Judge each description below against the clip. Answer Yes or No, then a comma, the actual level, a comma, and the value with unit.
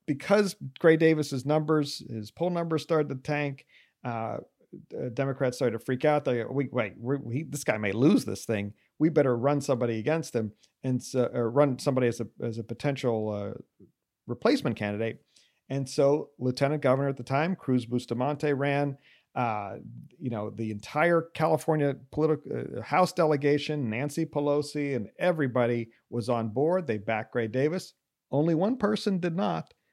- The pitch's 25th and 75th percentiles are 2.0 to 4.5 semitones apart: Yes, average, 4.2 semitones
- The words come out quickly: No, average, 165 wpm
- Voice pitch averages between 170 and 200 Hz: No, medium, 140 Hz